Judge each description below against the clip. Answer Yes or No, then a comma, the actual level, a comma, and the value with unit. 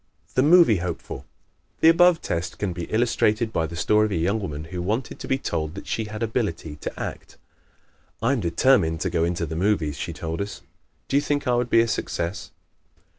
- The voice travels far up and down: Yes, wide, 6.0 semitones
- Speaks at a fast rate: Yes, fast, 220 wpm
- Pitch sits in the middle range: No, low, 100 Hz